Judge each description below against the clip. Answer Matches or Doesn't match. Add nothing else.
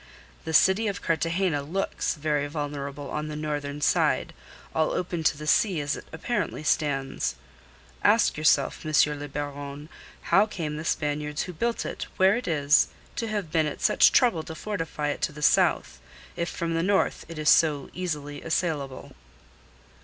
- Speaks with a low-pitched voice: Doesn't match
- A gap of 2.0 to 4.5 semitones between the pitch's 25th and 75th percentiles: Matches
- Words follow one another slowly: Doesn't match